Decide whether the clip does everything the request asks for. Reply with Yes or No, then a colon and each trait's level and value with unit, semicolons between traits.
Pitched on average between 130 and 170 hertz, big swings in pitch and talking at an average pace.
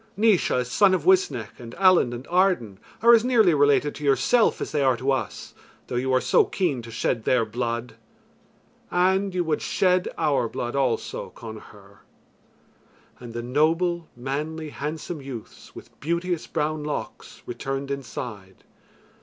Yes: medium, 140 Hz; wide, 6.3 semitones; average, 150 wpm